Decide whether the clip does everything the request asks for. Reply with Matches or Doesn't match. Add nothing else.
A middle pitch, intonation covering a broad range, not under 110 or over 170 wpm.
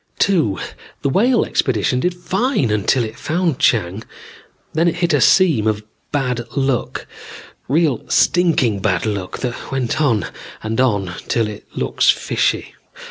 Doesn't match